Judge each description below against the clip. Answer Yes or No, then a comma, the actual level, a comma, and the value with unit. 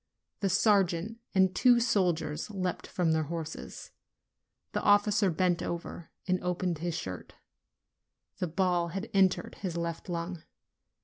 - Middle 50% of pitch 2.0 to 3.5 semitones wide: Yes, narrow, 2.5 semitones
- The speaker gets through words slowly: Yes, slow, 130 wpm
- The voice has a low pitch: No, medium, 180 Hz